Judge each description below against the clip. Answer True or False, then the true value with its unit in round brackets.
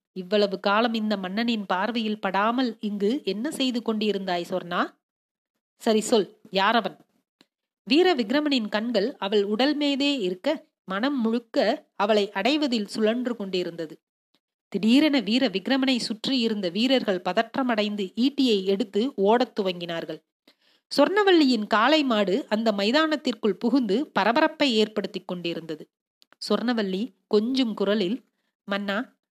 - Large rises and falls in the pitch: False (4.6 semitones)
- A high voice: True (220 Hz)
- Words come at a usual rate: True (100 wpm)